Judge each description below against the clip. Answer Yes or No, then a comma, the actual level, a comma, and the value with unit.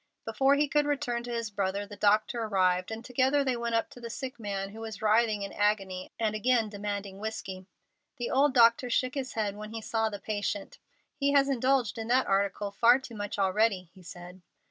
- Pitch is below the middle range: No, high, 220 Hz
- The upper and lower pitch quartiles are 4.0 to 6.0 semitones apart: No, average, 3.3 semitones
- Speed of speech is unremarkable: No, fast, 210 wpm